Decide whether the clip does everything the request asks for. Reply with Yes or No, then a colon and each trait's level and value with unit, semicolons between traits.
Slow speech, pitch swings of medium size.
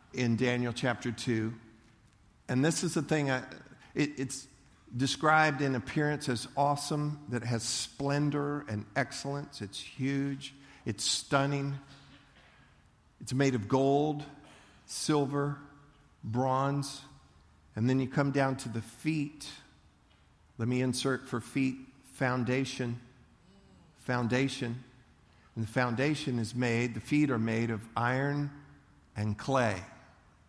Yes: slow, 120 wpm; average, 3.5 semitones